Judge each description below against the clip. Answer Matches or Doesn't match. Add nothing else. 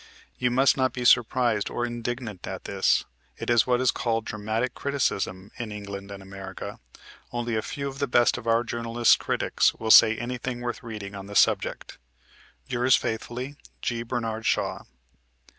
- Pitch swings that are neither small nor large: Doesn't match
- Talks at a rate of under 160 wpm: Doesn't match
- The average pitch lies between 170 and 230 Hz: Doesn't match